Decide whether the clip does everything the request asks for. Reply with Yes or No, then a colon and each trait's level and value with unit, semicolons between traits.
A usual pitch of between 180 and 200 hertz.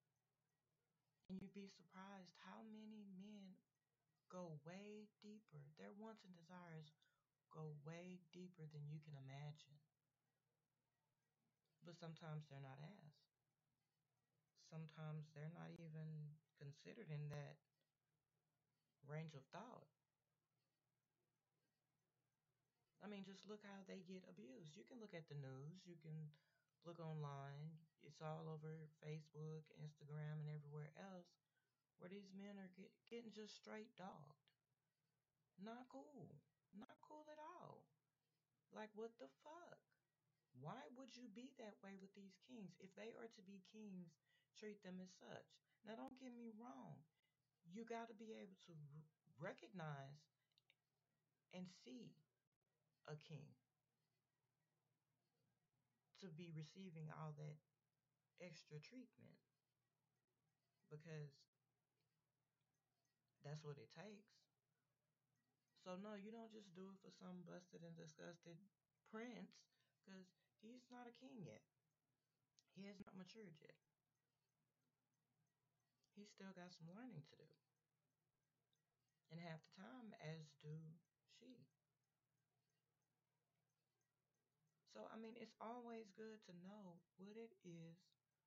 No: medium, 155 Hz